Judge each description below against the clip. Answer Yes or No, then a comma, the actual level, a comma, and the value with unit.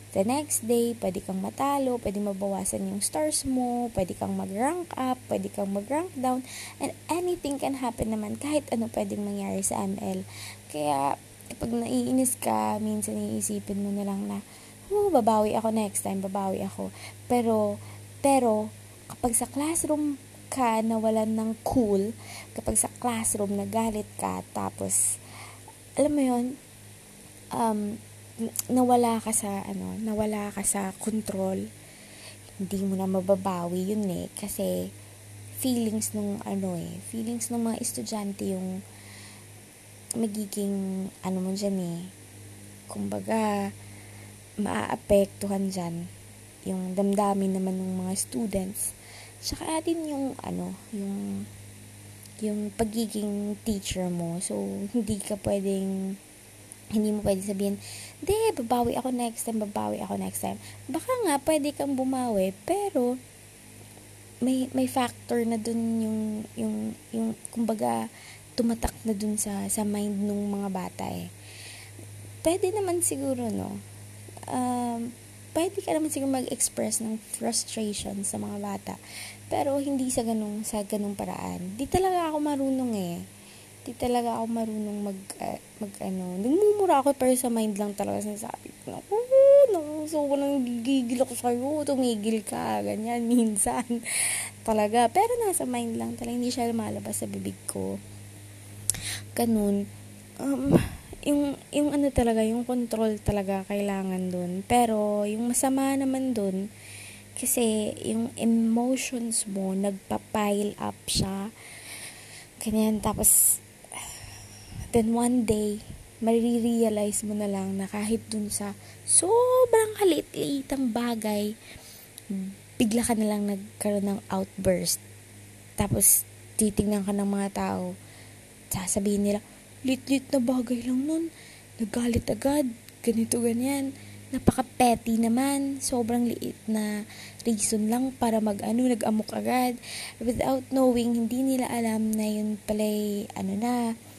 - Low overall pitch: No, high, 210 Hz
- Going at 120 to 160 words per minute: Yes, average, 125 wpm